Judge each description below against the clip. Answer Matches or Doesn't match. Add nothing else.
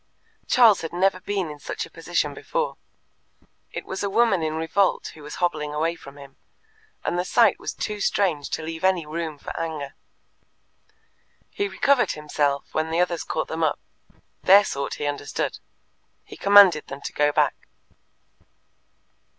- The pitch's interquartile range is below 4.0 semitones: Doesn't match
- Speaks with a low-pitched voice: Doesn't match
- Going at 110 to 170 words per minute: Matches